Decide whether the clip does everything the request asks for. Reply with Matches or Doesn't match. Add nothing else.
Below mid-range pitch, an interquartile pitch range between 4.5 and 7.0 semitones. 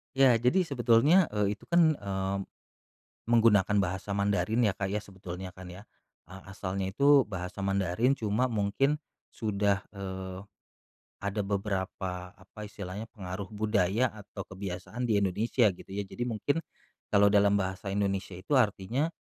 Doesn't match